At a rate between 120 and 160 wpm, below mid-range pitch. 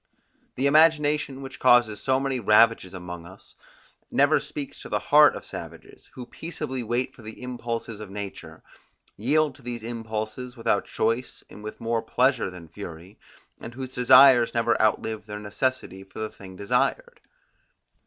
Yes: average, 155 wpm; low, 115 Hz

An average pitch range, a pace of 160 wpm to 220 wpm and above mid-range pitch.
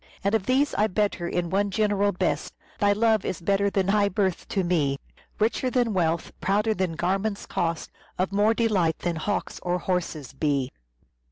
Yes: average, 3.3 semitones; average, 170 wpm; high, 195 Hz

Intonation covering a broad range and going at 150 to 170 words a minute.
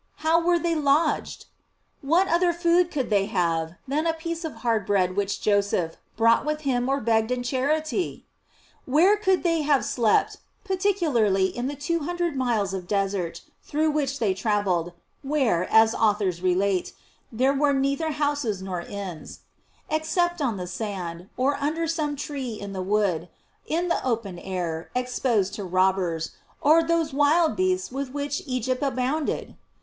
Yes: wide, 7.7 semitones; average, 160 wpm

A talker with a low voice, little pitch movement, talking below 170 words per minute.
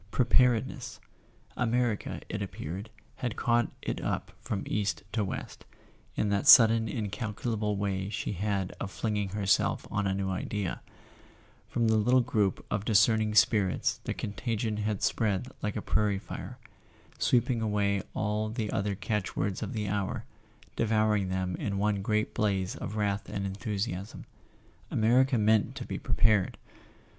Yes: low, 105 Hz; narrow, 2.0 semitones; average, 150 wpm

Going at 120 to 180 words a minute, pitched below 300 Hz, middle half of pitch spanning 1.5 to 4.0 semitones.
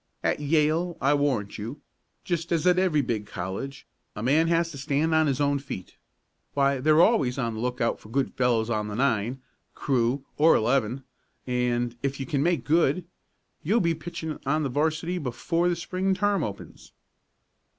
No: average, 175 wpm; medium, 140 Hz; average, 4.9 semitones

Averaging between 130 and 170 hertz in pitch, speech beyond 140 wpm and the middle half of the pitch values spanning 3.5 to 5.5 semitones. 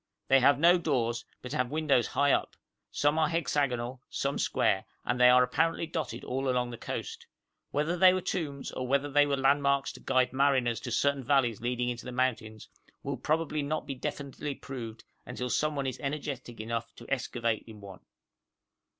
No: low, 135 Hz; average, 180 wpm; average, 3.0 semitones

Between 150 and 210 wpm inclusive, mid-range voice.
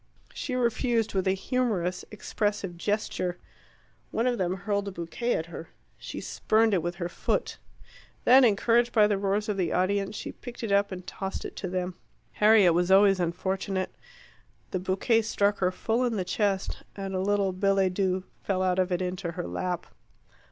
No: average, 180 wpm; high, 195 Hz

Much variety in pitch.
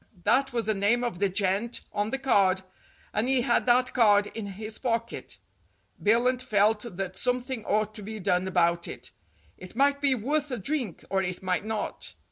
No: average, 4.1 semitones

